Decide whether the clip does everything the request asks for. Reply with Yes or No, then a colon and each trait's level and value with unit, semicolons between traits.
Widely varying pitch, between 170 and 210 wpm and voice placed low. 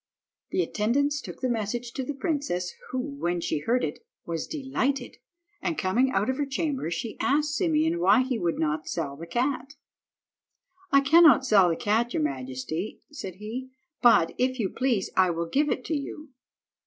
No: wide, 7.6 semitones; average, 180 wpm; very high, 250 Hz